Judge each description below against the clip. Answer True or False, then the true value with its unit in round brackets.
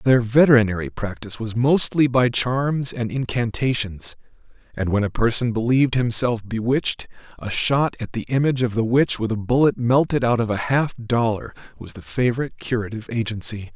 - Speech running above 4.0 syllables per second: True (5.4 syllables/s)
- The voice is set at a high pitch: False (120 Hz)